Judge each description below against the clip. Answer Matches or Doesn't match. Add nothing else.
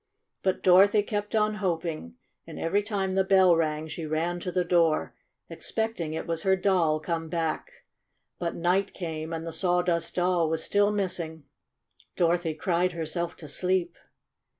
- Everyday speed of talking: Matches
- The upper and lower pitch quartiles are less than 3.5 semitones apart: Matches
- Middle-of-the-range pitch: Matches